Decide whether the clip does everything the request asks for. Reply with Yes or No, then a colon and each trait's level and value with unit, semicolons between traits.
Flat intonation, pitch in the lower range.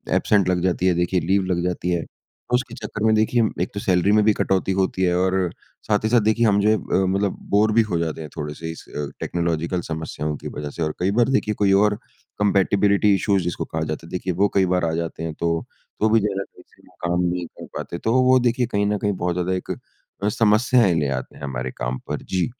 No: average, 3.7 semitones; very low, 95 Hz